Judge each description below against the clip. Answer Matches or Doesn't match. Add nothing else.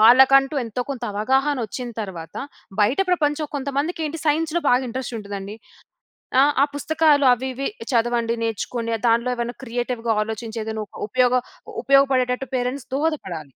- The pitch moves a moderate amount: Matches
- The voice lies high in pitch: Matches